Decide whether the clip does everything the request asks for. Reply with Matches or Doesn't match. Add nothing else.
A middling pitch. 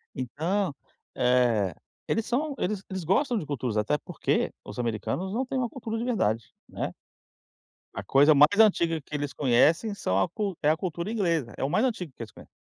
Matches